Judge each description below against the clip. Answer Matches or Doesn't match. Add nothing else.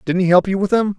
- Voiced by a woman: Doesn't match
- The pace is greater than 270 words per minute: Matches